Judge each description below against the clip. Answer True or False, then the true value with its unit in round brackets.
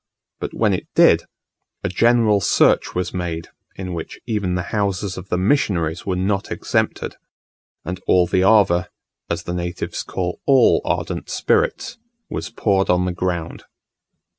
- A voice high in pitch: False (90 Hz)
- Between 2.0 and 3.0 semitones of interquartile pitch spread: True (2.7 semitones)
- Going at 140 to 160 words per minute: True (150 wpm)